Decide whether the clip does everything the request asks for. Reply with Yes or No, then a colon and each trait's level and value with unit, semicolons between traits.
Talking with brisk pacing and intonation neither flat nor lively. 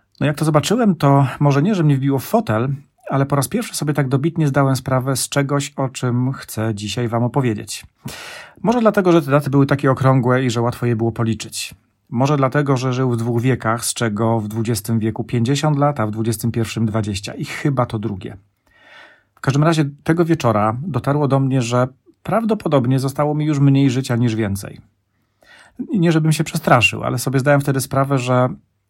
Yes: fast, 190 wpm; average, 3.9 semitones